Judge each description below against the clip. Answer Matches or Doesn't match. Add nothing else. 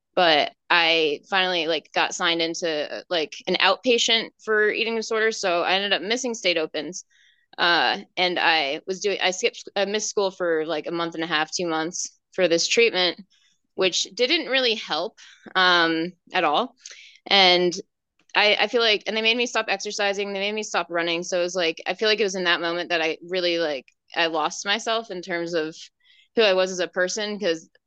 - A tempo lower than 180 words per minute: Doesn't match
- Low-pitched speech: Doesn't match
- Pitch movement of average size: Matches